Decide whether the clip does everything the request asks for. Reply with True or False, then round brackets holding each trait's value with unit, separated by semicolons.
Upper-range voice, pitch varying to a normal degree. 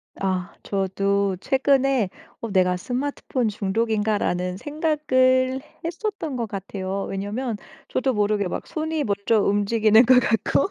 True (220 Hz; 4.8 semitones)